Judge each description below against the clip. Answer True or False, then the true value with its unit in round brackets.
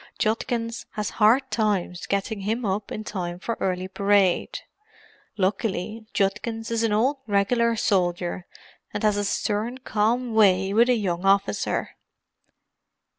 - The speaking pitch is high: True (210 Hz)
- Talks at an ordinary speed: False (130 wpm)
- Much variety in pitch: False (2.8 semitones)